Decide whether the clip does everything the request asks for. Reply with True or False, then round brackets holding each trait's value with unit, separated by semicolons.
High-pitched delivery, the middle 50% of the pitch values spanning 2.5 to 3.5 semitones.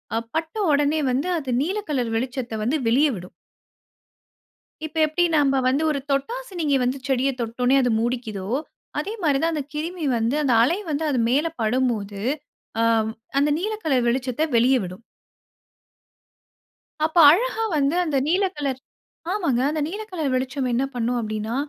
False (275 Hz; 4.3 semitones)